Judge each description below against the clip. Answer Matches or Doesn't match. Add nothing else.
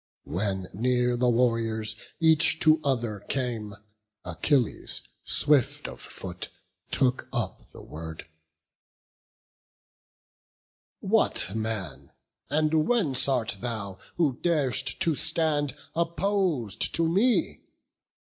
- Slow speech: Matches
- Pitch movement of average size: Doesn't match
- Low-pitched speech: Matches